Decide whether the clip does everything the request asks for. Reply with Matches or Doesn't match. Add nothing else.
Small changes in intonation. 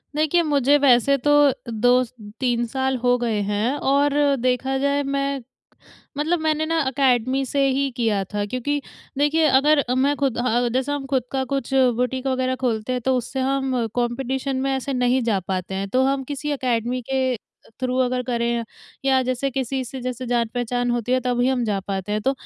Matches